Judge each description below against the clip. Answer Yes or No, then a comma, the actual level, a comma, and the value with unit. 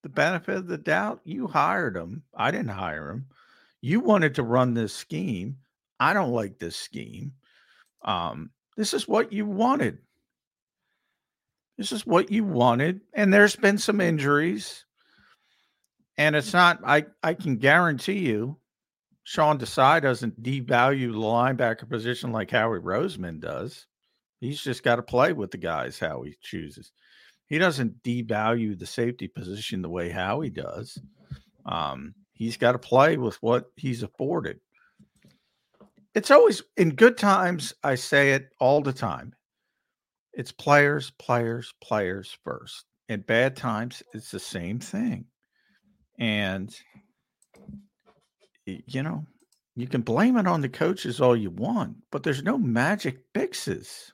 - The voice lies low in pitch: Yes, low, 130 Hz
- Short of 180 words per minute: Yes, average, 145 wpm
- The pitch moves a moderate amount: No, wide, 6.4 semitones